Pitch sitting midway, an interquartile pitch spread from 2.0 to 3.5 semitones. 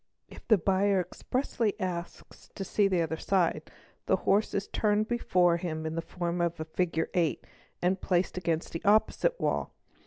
Yes: medium, 180 Hz; average, 2.9 semitones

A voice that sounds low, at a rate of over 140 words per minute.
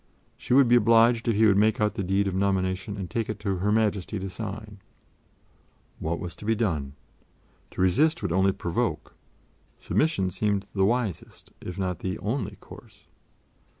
Yes: low, 100 Hz; average, 175 wpm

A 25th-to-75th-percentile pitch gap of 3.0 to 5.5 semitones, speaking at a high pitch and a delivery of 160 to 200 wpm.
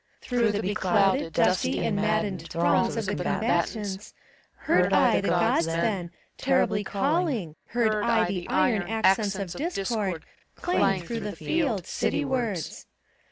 No: average, 3.8 semitones; high, 205 Hz; slow, 135 wpm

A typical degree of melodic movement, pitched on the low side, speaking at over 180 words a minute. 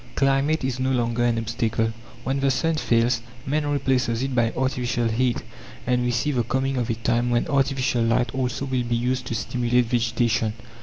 No: narrow, 2.2 semitones; low, 125 Hz; average, 190 wpm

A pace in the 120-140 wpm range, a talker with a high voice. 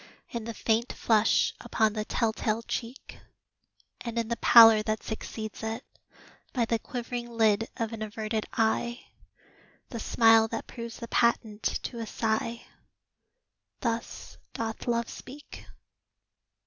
Yes: slow, 135 wpm; high, 230 Hz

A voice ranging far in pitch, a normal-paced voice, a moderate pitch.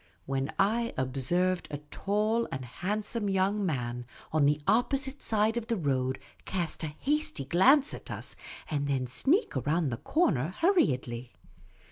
Yes: wide, 8.7 semitones; average, 150 wpm; medium, 175 Hz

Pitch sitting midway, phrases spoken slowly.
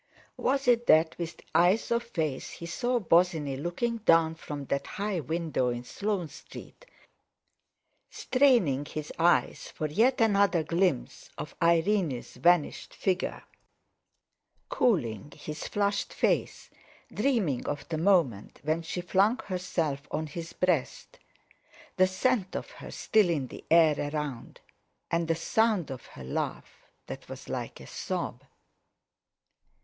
Yes: medium, 170 Hz; slow, 130 wpm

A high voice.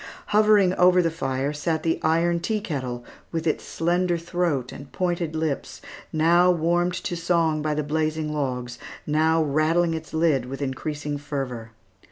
No: medium, 160 Hz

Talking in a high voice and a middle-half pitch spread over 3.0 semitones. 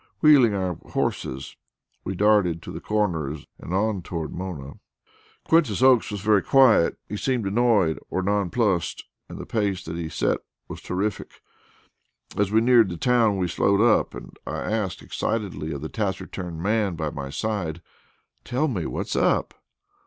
No: low, 100 Hz; average, 4.4 semitones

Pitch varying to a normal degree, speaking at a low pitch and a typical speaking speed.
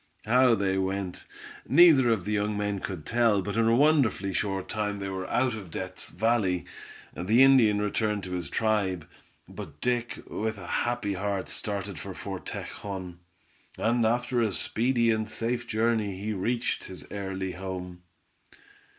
Yes: average, 3.5 semitones; low, 105 Hz; average, 160 wpm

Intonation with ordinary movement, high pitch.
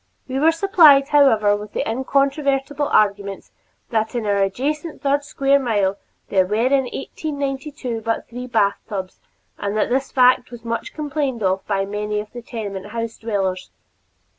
Yes: average, 5.0 semitones; high, 235 Hz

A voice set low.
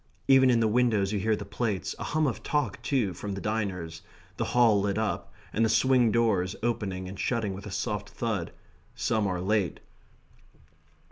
Yes: low, 105 Hz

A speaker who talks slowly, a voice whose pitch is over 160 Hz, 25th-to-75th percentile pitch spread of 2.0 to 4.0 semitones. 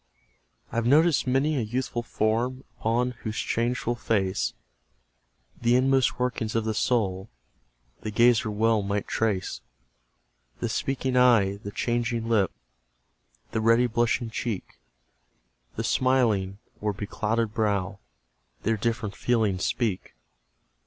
No: slow, 115 wpm; low, 115 Hz; average, 2.7 semitones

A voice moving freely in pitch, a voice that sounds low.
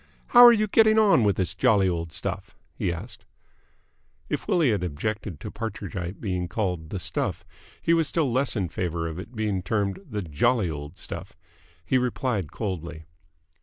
Yes: wide, 6.2 semitones; low, 100 Hz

